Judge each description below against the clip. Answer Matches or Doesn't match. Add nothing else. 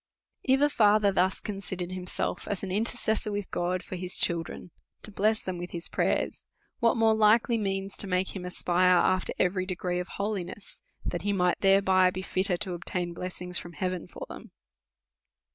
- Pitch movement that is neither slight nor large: Doesn't match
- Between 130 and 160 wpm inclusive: Doesn't match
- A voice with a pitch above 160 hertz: Matches